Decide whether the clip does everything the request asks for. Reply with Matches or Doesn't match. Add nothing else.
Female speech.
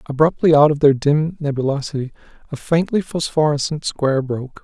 Doesn't match